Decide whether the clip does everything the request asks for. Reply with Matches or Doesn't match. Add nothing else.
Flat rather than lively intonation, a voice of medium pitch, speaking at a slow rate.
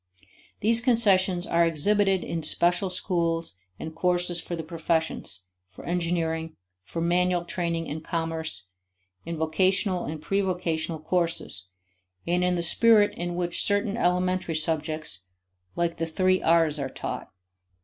Matches